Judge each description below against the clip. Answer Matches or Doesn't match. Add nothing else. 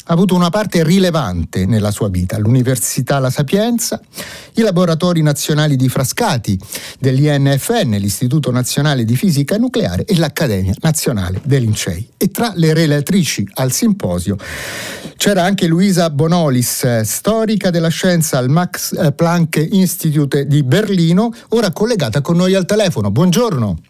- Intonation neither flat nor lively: Doesn't match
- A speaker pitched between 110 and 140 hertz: Doesn't match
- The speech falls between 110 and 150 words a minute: Matches